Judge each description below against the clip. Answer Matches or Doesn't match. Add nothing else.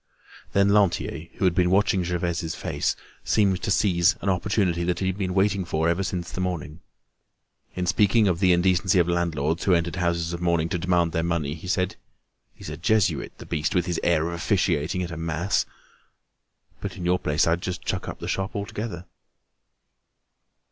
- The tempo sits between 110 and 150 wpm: Doesn't match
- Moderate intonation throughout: Doesn't match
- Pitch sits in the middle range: Doesn't match